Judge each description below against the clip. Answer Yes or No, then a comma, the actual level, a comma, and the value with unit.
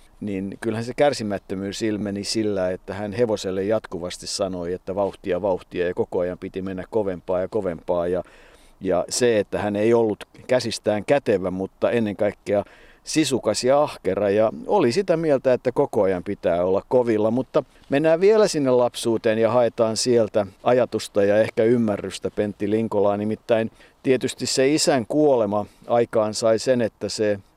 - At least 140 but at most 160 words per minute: Yes, fast, 155 wpm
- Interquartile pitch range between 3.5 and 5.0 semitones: Yes, average, 3.8 semitones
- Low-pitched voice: Yes, low, 110 Hz